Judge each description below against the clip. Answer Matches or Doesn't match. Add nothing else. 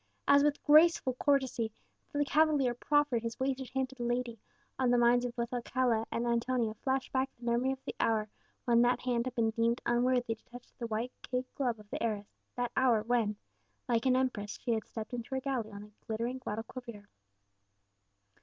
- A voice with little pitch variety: Matches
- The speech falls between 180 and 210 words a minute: Matches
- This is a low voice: Doesn't match